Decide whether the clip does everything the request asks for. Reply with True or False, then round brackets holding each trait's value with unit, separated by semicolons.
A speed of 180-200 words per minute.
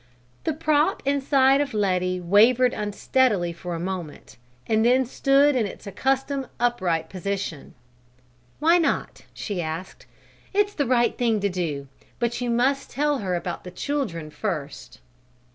False (145 wpm)